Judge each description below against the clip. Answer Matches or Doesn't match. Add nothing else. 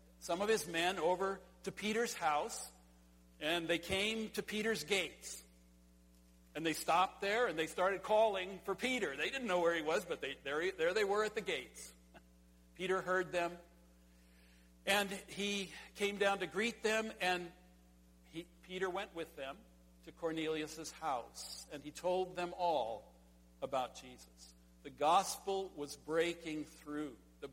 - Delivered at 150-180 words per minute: Matches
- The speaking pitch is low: Doesn't match